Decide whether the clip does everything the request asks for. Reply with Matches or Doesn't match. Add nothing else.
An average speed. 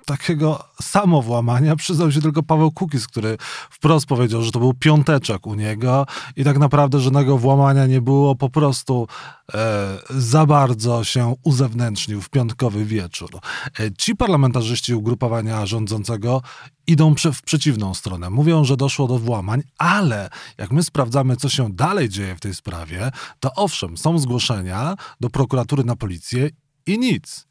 Matches